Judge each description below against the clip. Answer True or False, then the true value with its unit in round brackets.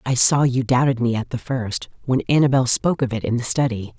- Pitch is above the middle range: False (125 Hz)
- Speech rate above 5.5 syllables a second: True (5.8 syllables/s)